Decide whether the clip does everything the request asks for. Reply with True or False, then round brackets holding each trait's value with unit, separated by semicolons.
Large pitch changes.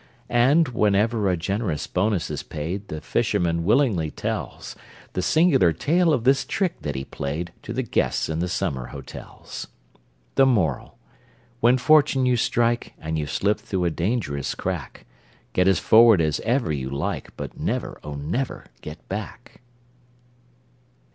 True (7.6 semitones)